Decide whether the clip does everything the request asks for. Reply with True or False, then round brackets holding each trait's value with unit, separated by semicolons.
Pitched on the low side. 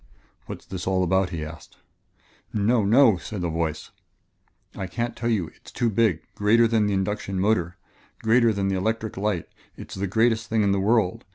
True (100 Hz)